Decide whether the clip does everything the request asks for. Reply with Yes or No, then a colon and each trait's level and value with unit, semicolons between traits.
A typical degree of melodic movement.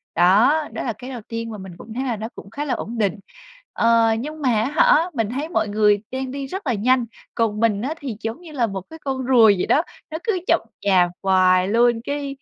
Yes: average, 4.4 semitones